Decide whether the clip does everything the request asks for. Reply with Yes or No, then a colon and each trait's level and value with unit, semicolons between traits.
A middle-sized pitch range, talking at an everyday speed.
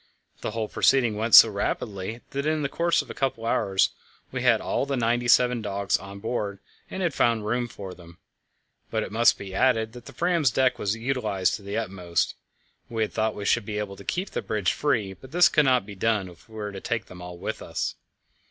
No: average, 3.9 semitones; fast, 230 wpm